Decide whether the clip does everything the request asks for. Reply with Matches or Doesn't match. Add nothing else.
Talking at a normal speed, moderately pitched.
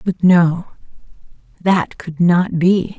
Doesn't match